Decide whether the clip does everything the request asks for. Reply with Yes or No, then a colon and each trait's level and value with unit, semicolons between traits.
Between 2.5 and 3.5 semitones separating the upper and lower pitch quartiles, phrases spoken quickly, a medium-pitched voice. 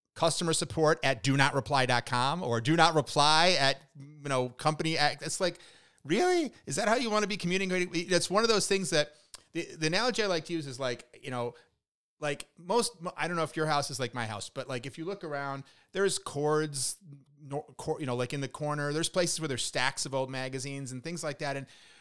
No: average, 3.9 semitones; fast, 225 wpm; medium, 150 Hz